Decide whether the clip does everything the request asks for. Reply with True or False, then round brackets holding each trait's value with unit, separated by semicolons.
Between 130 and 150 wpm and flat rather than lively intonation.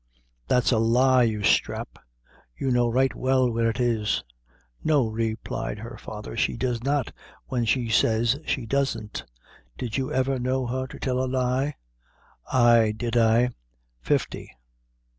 True (145 wpm; 2.3 semitones)